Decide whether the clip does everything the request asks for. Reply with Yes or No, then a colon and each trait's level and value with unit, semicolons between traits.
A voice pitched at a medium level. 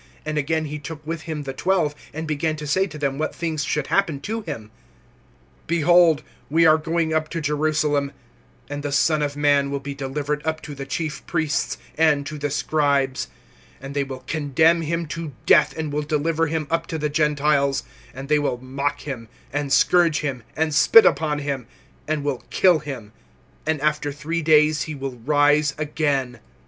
Yes: medium, 150 Hz